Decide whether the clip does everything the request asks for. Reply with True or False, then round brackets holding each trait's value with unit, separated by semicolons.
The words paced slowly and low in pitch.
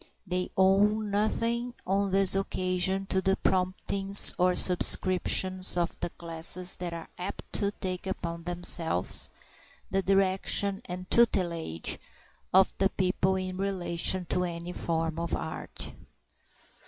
False (130 wpm; 185 Hz)